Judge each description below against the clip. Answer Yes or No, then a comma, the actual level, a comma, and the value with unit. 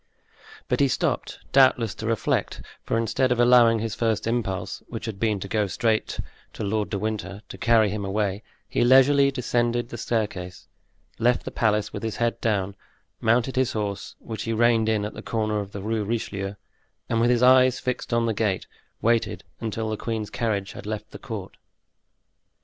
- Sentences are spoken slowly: No, average, 185 wpm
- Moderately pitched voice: No, low, 110 Hz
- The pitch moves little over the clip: Yes, narrow, 2.2 semitones